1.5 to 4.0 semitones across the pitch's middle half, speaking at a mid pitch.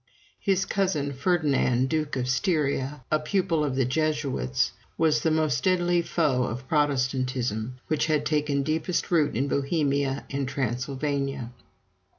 Yes: average, 3.2 semitones; medium, 145 Hz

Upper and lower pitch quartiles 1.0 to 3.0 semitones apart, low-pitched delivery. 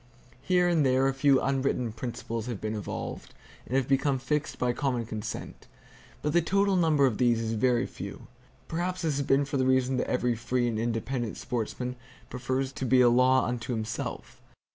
Yes: narrow, 2.6 semitones; low, 130 Hz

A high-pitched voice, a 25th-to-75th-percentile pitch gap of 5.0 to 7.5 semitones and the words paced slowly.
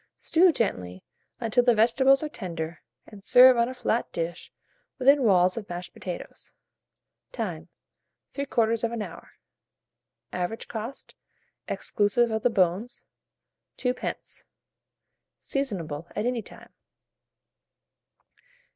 Yes: high, 225 Hz; wide, 5.5 semitones; slow, 100 wpm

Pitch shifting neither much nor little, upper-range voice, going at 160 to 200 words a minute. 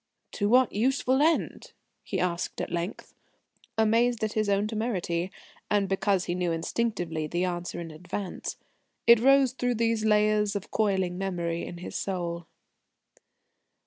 No: average, 4.2 semitones; high, 200 Hz; average, 145 wpm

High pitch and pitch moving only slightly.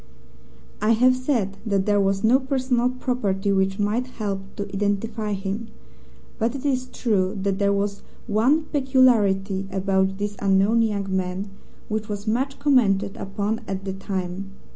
No: high, 205 Hz; average, 3.7 semitones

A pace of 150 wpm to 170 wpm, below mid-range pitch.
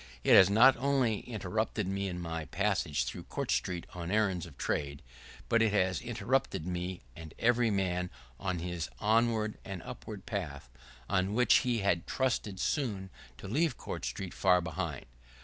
Yes: average, 165 wpm; very low, 95 Hz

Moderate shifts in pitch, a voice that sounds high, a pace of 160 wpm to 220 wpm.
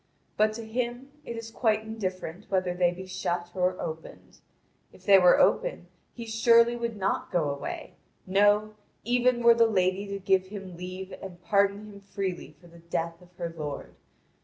Yes: average, 3.7 semitones; high, 195 Hz; average, 175 wpm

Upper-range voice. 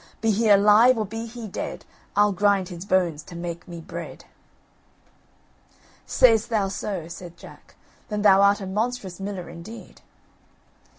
Yes: high, 200 Hz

